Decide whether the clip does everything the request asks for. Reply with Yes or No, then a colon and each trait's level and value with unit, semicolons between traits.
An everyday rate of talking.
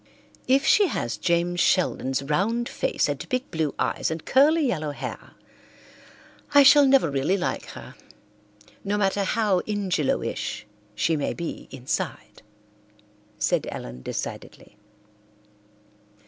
No: slow, 120 wpm